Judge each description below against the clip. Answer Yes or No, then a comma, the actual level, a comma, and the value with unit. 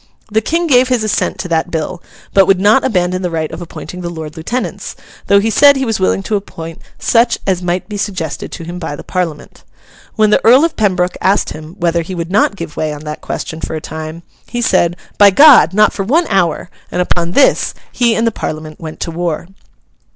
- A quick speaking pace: Yes, fast, 220 wpm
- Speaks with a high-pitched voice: No, medium, 180 Hz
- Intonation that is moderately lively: Yes, average, 4.6 semitones